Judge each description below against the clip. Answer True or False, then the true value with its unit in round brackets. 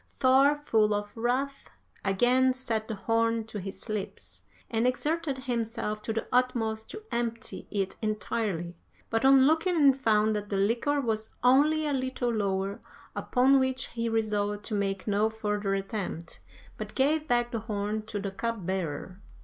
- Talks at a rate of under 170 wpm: True (155 wpm)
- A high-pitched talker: True (225 Hz)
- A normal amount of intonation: True (3.9 semitones)